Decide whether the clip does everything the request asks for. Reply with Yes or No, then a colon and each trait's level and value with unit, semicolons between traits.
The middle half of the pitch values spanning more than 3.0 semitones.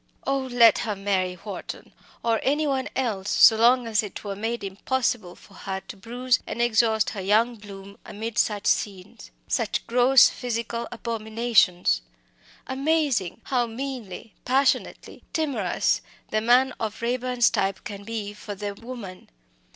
Yes: average, 3.5 semitones